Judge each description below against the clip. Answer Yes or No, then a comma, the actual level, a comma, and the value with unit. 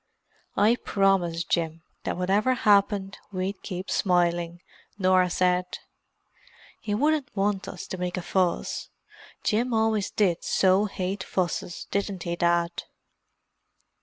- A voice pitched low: No, medium, 185 Hz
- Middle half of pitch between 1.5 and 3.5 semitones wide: Yes, narrow, 2.6 semitones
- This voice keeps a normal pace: No, slow, 120 wpm